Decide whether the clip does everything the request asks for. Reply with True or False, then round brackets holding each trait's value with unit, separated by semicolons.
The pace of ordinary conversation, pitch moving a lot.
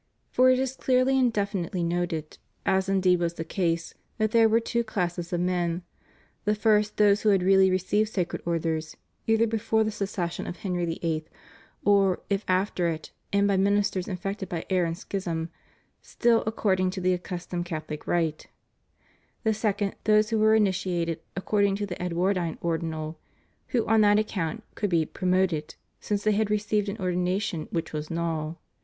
False (170 wpm; 3.6 semitones)